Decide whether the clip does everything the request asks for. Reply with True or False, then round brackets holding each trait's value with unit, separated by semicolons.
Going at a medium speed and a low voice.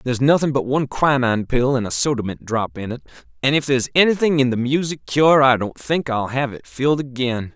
False (230 wpm; 130 Hz)